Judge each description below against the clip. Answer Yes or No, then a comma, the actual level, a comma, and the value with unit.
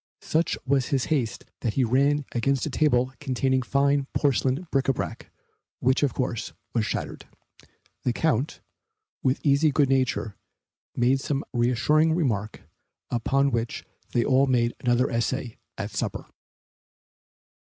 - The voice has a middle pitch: No, low, 130 Hz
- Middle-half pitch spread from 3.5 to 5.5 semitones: No, narrow, 2.6 semitones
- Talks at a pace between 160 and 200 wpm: No, average, 140 wpm